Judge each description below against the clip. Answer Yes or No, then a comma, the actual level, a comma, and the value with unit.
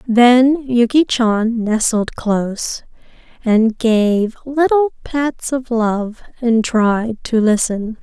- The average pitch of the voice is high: Yes, high, 235 Hz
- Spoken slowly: Yes, slow, 110 wpm